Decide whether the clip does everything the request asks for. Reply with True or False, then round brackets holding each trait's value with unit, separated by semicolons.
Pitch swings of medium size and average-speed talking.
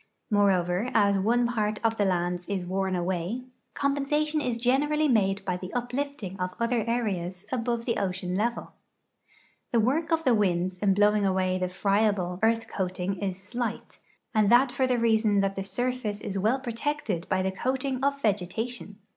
True (4.5 semitones; 170 wpm)